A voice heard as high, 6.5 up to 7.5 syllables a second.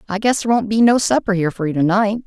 Yes: high, 210 Hz; 7.2 syllables/s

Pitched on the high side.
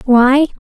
Yes: very high, 265 Hz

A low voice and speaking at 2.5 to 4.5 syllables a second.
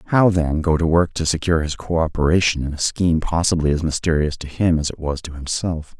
No: very low, 80 Hz; 5.6 syllables/s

